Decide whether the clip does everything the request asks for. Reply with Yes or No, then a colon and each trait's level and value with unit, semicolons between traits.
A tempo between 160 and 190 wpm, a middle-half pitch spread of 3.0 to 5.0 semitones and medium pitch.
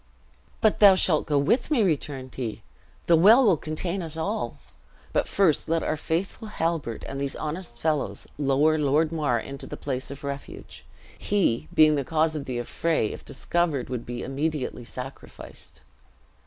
Yes: average, 165 wpm; average, 3.6 semitones; medium, 155 Hz